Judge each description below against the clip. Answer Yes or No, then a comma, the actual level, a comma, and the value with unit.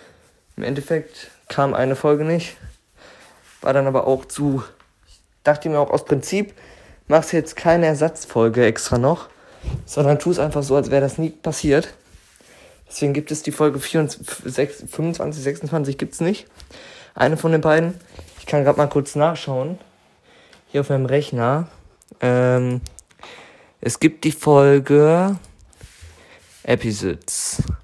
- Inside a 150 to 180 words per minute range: No, average, 135 wpm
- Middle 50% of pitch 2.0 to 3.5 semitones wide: Yes, average, 3.2 semitones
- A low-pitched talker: No, medium, 145 Hz